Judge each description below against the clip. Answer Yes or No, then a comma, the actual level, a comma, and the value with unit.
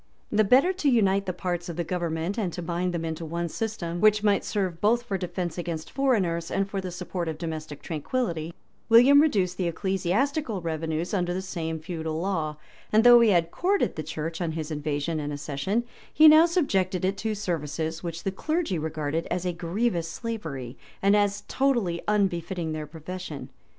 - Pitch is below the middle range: No, medium, 180 Hz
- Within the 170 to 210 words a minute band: Yes, average, 185 wpm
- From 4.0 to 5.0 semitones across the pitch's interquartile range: Yes, average, 4.3 semitones